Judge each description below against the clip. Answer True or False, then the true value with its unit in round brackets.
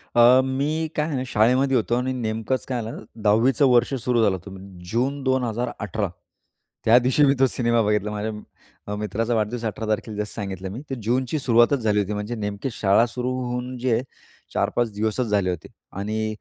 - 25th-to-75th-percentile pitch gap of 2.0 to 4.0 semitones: True (3.3 semitones)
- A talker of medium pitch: False (115 Hz)